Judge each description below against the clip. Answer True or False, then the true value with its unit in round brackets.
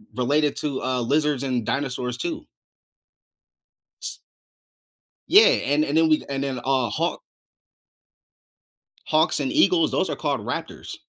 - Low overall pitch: False (145 Hz)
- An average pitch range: True (3.4 semitones)